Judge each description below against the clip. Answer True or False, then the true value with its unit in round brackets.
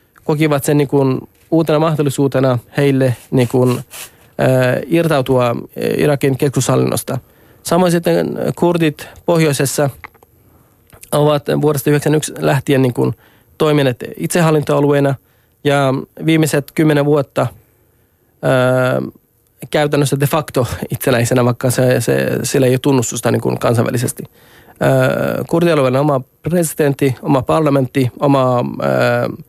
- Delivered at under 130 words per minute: True (100 wpm)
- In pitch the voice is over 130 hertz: True (140 Hz)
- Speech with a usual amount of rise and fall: True (3.3 semitones)